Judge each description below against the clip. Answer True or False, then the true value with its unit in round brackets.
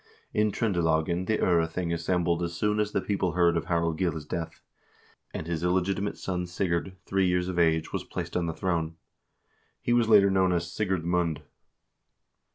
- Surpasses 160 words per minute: True (170 wpm)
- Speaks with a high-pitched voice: False (90 Hz)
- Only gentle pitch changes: True (2.3 semitones)